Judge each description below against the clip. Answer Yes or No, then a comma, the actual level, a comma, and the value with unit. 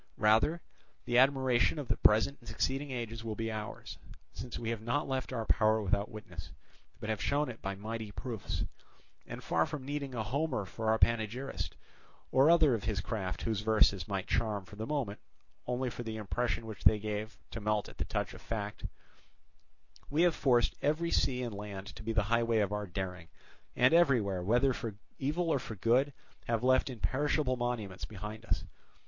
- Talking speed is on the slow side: No, average, 190 wpm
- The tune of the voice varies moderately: Yes, average, 3.7 semitones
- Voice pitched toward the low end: Yes, low, 115 Hz